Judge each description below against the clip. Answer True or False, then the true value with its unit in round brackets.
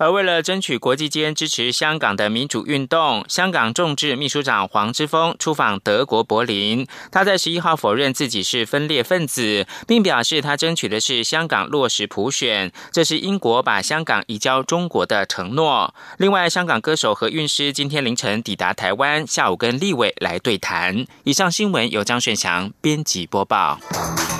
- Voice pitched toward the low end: False (145 Hz)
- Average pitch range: False (6.1 semitones)